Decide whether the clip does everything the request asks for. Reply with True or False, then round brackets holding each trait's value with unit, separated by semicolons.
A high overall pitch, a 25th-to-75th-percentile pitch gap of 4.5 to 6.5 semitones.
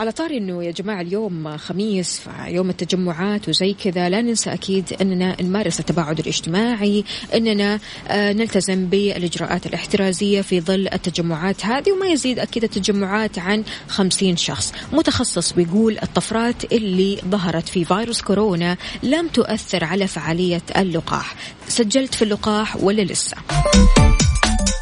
False (195 Hz; 3.4 semitones)